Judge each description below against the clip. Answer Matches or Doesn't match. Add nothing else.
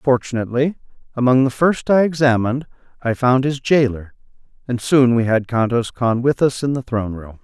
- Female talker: Doesn't match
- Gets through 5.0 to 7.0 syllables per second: Matches